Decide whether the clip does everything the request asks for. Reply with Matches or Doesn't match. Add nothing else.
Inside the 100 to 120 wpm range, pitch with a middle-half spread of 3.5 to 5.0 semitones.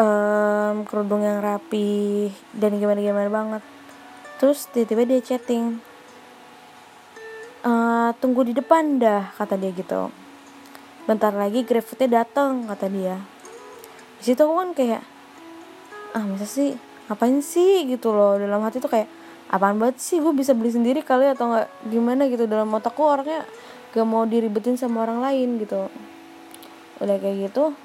Doesn't match